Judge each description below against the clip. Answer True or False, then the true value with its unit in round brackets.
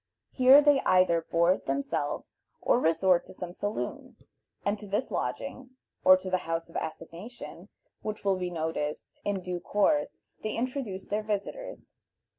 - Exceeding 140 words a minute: True (150 wpm)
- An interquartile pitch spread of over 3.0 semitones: True (4.5 semitones)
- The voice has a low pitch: False (190 Hz)